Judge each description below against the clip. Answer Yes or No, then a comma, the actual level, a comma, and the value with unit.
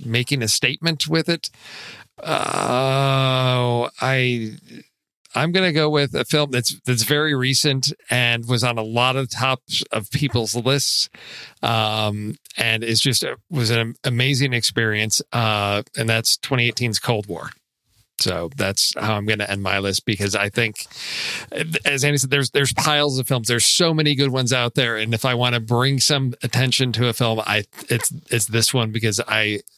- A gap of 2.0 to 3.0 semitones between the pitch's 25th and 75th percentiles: No, average, 3.4 semitones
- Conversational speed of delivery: Yes, average, 175 wpm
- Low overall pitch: Yes, low, 125 Hz